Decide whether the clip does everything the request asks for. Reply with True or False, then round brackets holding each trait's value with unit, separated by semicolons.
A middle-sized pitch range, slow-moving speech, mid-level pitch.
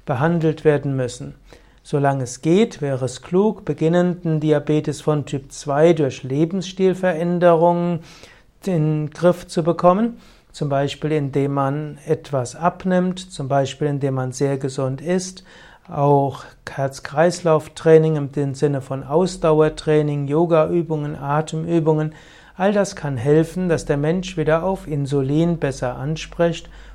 True (3.3 semitones; 120 wpm; 155 Hz)